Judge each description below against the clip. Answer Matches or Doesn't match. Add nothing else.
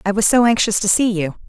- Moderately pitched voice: Doesn't match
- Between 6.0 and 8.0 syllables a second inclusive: Matches